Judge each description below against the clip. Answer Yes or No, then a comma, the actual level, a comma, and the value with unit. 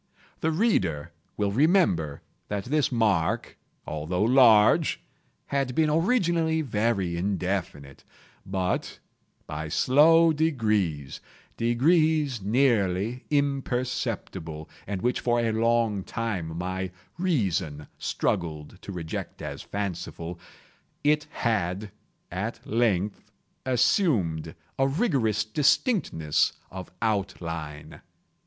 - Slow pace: Yes, slow, 90 wpm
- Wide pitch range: Yes, wide, 7.3 semitones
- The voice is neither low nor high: No, low, 110 Hz